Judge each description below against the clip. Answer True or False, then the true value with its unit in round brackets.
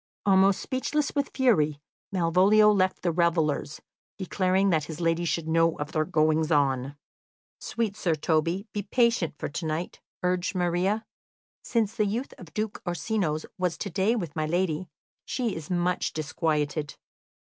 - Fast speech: False (150 wpm)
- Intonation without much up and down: False (4.2 semitones)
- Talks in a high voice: False (175 Hz)